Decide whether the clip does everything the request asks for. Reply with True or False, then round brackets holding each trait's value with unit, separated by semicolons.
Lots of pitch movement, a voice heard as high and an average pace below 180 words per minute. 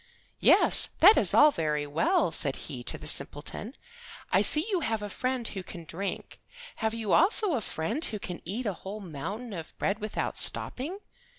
False (7.6 semitones; 210 Hz; 185 wpm)